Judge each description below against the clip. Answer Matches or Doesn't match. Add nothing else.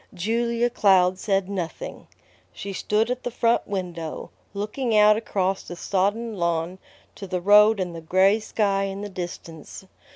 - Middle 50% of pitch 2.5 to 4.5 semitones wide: Matches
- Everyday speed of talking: Matches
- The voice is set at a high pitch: Matches